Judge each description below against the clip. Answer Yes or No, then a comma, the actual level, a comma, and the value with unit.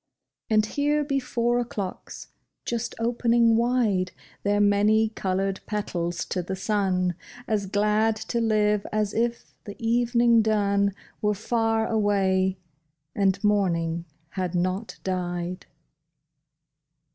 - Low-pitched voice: No, high, 210 Hz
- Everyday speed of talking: No, slow, 110 wpm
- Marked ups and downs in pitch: No, average, 3.2 semitones